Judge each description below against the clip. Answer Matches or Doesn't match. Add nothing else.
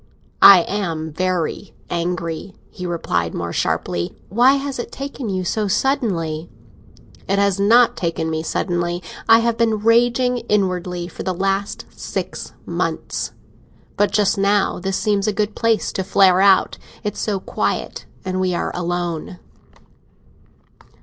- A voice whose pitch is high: Matches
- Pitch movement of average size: Matches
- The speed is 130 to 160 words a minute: Matches